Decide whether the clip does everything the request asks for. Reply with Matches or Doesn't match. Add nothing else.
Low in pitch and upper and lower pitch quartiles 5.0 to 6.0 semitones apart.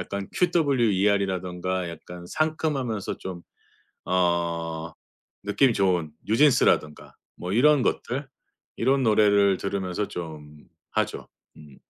Matches